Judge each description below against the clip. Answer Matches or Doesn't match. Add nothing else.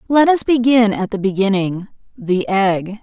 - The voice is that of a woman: Matches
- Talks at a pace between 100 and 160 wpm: Matches